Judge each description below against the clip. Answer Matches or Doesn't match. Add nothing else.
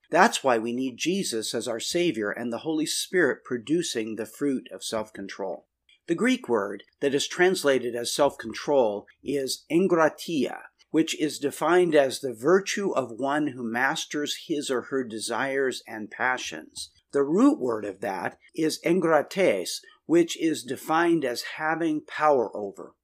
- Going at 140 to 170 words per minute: Matches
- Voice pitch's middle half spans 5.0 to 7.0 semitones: Matches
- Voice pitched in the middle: Matches